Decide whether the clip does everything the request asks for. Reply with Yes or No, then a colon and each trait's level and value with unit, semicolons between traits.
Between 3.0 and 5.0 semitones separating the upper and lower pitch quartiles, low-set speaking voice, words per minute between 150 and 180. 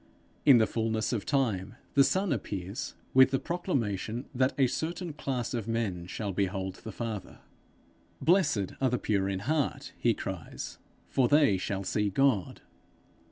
No: wide, 5.6 semitones; low, 115 Hz; average, 155 wpm